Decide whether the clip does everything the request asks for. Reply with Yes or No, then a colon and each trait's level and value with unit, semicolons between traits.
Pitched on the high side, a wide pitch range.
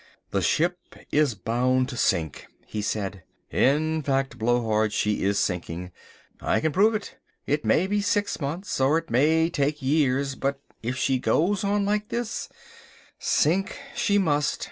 No: medium, 145 Hz; wide, 6.5 semitones